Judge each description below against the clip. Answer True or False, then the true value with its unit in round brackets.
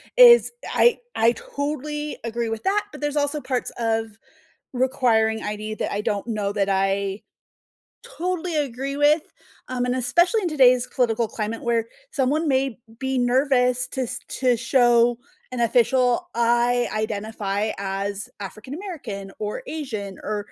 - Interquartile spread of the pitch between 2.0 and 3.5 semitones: False (4.3 semitones)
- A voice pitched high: True (245 Hz)